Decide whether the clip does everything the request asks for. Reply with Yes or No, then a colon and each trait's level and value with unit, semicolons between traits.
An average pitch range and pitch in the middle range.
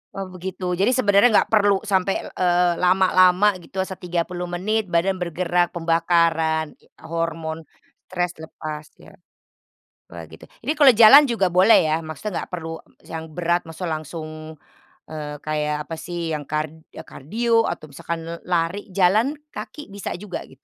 Yes: average, 3.1 semitones; medium, 175 Hz